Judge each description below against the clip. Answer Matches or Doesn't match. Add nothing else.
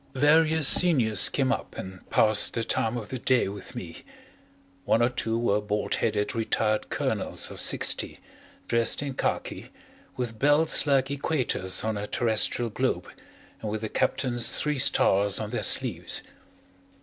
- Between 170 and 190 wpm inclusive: Doesn't match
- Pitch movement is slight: Doesn't match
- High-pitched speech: Doesn't match